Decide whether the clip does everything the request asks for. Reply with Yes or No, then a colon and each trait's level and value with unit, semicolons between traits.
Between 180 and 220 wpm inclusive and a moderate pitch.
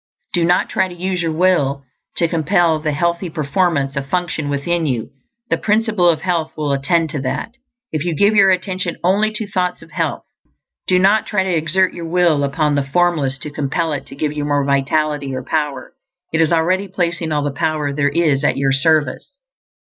Yes: average, 200 wpm; medium, 160 Hz